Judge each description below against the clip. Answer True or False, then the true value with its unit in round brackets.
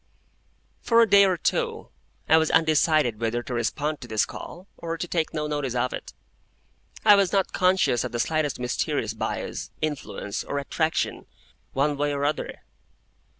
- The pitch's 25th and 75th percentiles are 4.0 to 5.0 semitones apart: True (4.7 semitones)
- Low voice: False (150 Hz)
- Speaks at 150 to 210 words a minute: True (160 wpm)